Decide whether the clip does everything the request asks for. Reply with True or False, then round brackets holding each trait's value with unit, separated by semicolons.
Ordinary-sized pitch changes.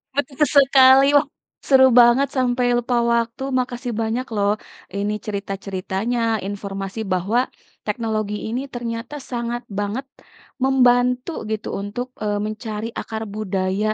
True (3.3 semitones)